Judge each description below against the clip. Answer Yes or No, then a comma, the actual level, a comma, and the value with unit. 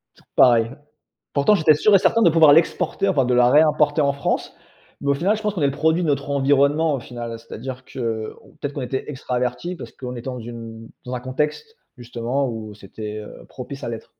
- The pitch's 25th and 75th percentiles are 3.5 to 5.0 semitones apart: Yes, average, 4.2 semitones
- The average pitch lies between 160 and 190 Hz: No, low, 135 Hz